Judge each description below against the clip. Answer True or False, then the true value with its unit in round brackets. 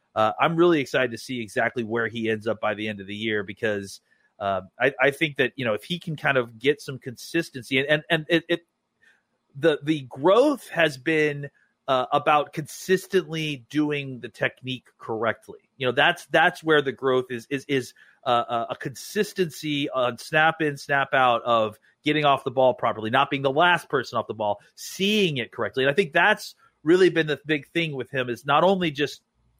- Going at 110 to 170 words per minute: False (205 wpm)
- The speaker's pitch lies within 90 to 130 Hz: False (140 Hz)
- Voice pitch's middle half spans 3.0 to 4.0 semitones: False (5.0 semitones)